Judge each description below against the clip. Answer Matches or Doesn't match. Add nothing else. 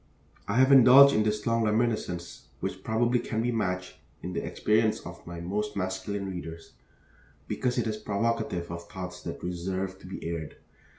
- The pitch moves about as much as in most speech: Matches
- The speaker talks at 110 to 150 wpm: Doesn't match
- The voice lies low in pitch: Matches